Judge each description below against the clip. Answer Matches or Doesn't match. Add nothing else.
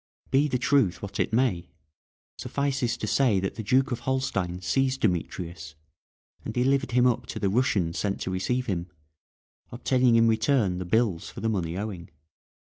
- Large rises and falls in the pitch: Matches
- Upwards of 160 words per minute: Matches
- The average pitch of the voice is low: Matches